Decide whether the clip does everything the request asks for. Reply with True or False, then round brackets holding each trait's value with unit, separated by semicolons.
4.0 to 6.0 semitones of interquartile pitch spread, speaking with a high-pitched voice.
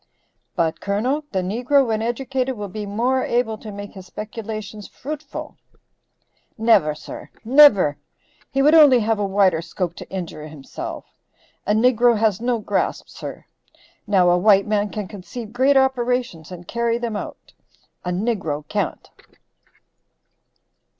True (4.4 semitones; 215 Hz)